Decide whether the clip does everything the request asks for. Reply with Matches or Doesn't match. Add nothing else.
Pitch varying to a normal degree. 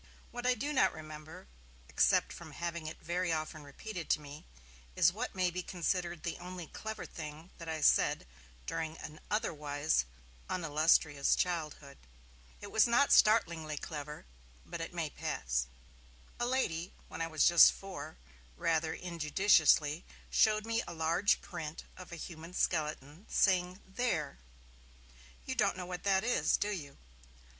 Matches